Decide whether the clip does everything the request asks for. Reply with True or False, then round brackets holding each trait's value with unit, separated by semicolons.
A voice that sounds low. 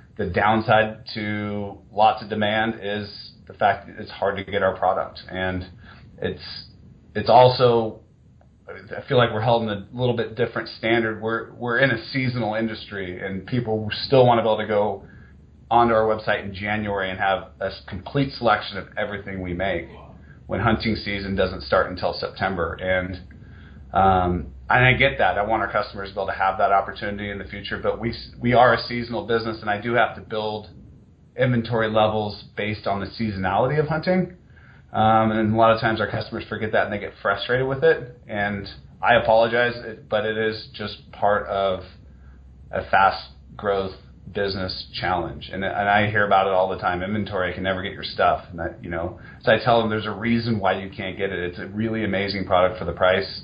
True (105 Hz)